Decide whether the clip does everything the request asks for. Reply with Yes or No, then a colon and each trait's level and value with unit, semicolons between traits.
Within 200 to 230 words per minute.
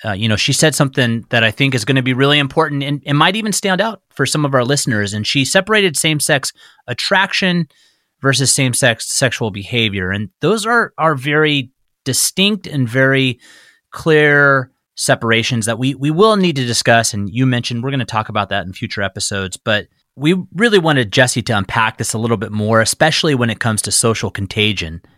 Yes: fast, 205 wpm